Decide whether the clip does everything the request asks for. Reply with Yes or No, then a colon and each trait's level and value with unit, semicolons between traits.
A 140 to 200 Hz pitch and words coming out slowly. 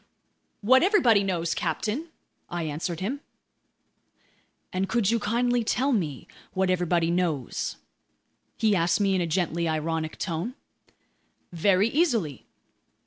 Yes: medium, 185 Hz; slow, 120 wpm